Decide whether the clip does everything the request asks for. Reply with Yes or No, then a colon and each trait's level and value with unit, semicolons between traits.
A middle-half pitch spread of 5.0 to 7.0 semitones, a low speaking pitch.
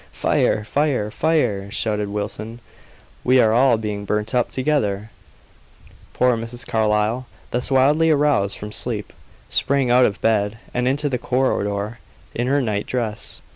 No: average, 3.7 semitones; low, 115 Hz